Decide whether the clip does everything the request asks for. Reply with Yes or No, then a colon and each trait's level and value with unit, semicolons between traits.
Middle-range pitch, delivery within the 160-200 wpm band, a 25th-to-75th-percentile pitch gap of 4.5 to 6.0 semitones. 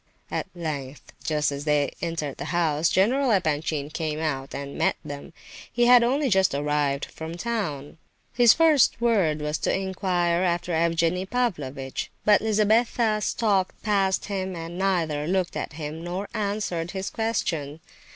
No: medium, 175 Hz; average, 150 wpm; average, 5.3 semitones